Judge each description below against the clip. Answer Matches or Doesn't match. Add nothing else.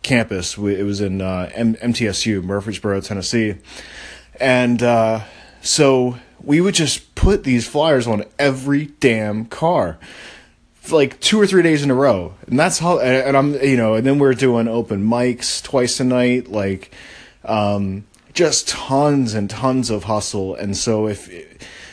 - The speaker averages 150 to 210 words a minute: Matches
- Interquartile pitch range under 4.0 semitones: Doesn't match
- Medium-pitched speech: Doesn't match